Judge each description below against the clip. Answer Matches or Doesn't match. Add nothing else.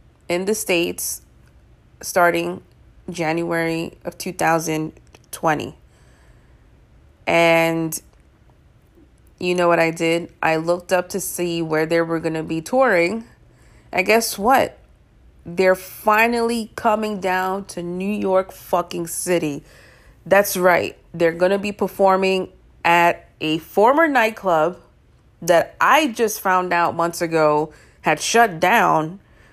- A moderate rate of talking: Doesn't match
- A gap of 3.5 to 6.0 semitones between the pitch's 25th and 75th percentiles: Doesn't match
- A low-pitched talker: Doesn't match